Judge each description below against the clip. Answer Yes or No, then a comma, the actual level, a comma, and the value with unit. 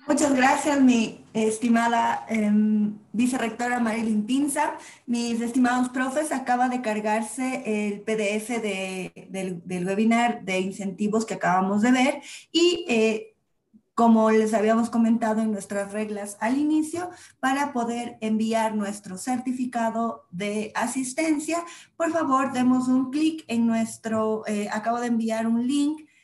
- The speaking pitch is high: Yes, high, 230 Hz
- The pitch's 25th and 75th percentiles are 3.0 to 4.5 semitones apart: Yes, average, 3.3 semitones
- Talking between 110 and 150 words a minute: Yes, average, 130 wpm